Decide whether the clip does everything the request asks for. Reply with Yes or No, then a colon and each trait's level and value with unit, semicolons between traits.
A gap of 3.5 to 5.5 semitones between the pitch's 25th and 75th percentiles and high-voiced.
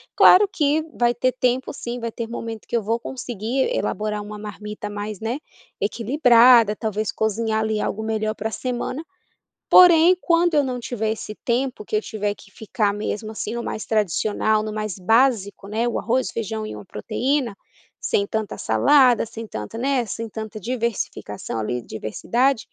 No: average, 2.7 semitones; high, 220 Hz